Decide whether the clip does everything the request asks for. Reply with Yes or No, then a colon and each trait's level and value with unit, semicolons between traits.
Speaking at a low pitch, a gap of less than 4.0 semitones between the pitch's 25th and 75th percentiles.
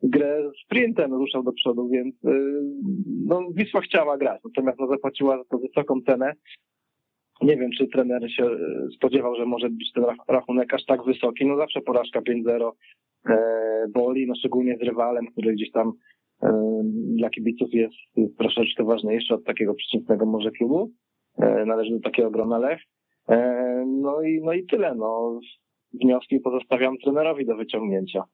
Yes: low, 125 Hz; average, 2.8 semitones